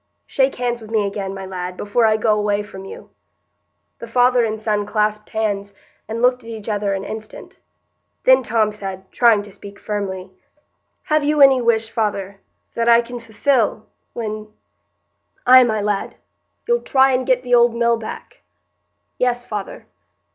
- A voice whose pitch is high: Yes, high, 220 Hz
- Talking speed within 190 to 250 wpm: No, average, 160 wpm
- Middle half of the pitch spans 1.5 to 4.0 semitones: Yes, average, 2.9 semitones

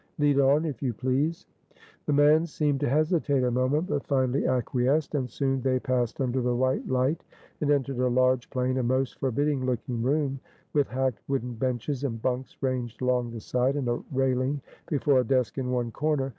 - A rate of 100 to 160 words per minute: No, average, 190 wpm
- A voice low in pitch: Yes, low, 130 Hz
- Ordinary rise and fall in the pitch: No, narrow, 2.2 semitones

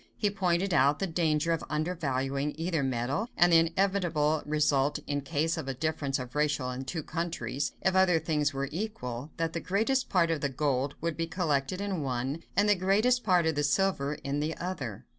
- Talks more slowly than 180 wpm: No, average, 200 wpm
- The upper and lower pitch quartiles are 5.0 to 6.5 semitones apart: No, average, 4.3 semitones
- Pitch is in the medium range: Yes, medium, 160 Hz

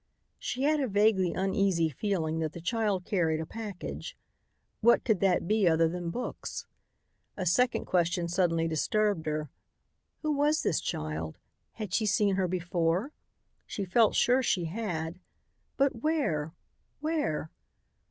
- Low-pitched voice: No, medium, 185 Hz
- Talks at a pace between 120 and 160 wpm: Yes, average, 140 wpm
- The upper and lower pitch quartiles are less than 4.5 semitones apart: No, average, 5.2 semitones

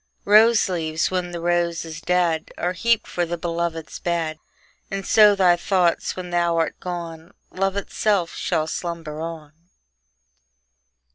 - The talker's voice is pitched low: No, medium, 175 Hz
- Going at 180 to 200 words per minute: No, average, 140 wpm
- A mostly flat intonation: Yes, narrow, 1.9 semitones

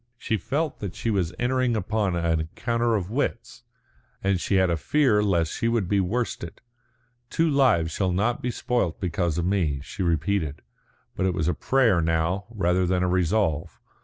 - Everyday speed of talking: Yes, average, 180 wpm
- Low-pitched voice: Yes, very low, 95 Hz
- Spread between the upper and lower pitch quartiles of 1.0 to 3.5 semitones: No, average, 5.2 semitones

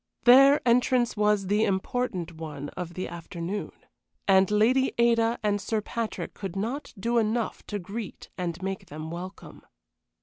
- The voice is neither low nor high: No, high, 205 Hz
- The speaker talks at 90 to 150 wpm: Yes, average, 145 wpm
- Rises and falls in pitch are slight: No, average, 4.4 semitones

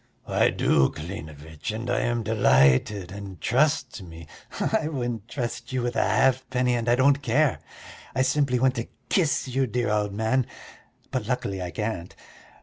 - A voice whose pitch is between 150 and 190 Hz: No, low, 120 Hz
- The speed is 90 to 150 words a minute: No, average, 160 wpm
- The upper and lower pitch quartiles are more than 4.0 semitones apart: Yes, average, 4.6 semitones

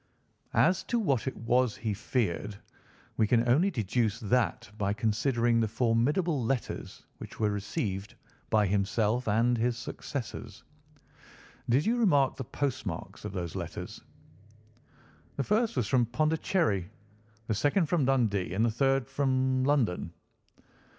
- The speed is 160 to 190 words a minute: No, slow, 135 wpm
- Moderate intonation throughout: Yes, average, 4.2 semitones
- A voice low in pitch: Yes, low, 120 Hz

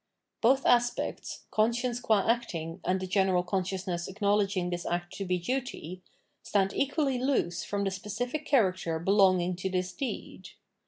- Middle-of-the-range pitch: No, high, 195 Hz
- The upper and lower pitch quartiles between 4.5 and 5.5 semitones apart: Yes, average, 4.8 semitones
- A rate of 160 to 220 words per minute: No, average, 145 wpm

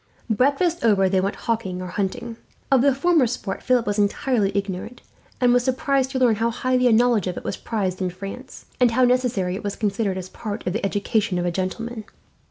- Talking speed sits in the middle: No, fast, 210 wpm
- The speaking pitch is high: Yes, high, 225 Hz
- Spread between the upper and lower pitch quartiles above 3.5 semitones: Yes, average, 4.4 semitones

